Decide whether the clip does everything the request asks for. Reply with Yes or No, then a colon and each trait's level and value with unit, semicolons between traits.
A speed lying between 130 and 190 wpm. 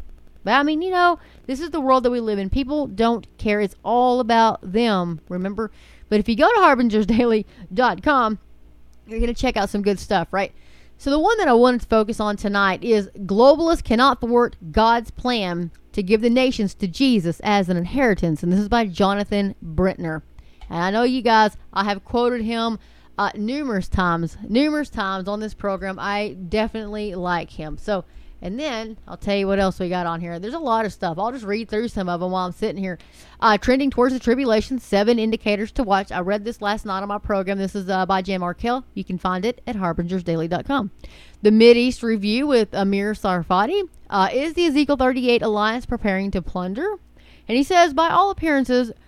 No: fast, 205 wpm